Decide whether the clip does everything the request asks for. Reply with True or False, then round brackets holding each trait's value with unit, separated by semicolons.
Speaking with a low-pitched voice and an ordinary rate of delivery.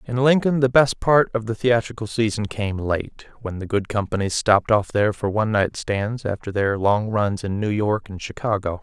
False (110 Hz; 210 wpm)